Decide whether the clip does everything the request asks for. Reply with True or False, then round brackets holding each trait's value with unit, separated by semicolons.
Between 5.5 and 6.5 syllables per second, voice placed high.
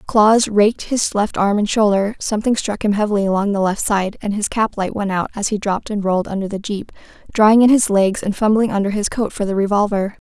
True (5.9 syllables/s; 205 Hz)